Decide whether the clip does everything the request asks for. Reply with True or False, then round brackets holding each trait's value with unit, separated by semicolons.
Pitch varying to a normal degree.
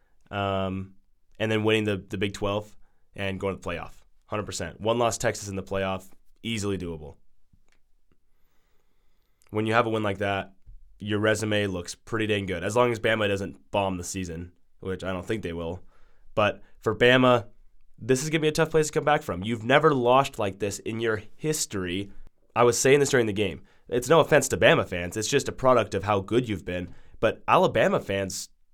True (3.3 semitones)